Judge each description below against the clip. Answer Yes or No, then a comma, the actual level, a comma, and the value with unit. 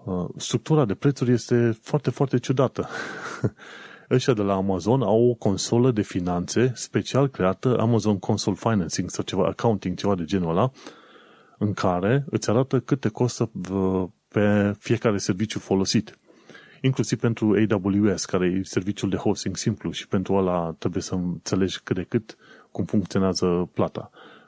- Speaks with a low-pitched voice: Yes, low, 105 Hz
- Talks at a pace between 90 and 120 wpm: No, average, 145 wpm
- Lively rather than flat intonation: No, average, 4.2 semitones